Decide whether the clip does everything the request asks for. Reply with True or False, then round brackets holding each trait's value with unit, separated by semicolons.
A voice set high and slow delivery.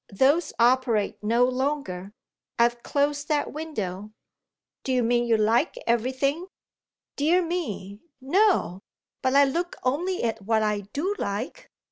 True (255 Hz; 130 wpm)